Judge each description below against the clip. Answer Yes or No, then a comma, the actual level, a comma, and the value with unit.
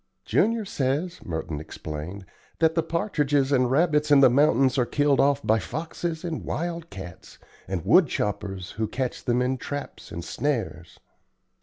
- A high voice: No, low, 135 Hz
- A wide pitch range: Yes, wide, 7.4 semitones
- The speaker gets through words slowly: No, average, 155 wpm